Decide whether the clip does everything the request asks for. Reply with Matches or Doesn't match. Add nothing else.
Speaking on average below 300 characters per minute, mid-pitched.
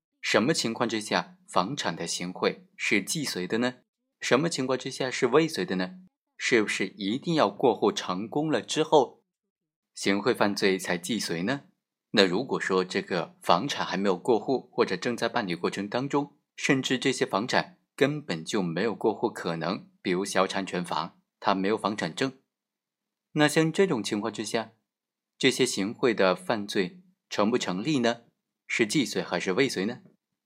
Doesn't match